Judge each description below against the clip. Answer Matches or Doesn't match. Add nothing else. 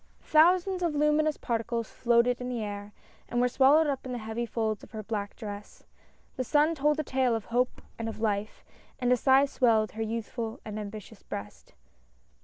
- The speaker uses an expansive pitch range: Doesn't match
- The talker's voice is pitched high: Matches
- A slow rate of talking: Doesn't match